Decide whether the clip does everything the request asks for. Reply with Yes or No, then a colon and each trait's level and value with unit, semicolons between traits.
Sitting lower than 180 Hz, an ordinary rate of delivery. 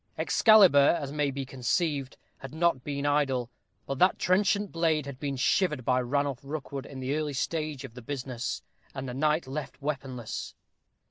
Yes: medium, 140 Hz; average, 170 wpm